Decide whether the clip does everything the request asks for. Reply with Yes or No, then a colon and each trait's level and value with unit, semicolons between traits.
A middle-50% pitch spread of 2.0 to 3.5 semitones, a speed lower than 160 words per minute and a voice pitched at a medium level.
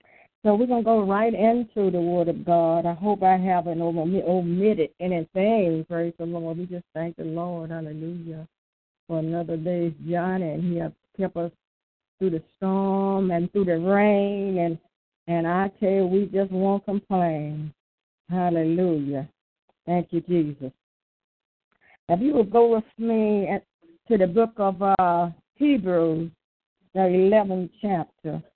Yes: average, 2.9 semitones; average, 150 wpm; medium, 180 Hz